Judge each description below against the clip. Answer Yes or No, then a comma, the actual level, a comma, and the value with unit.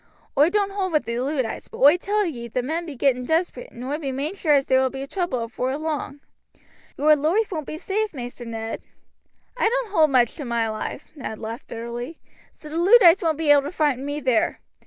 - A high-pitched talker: Yes, very high, 290 Hz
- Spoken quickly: Yes, fast, 220 wpm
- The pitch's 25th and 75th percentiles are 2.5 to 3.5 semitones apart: No, average, 5.1 semitones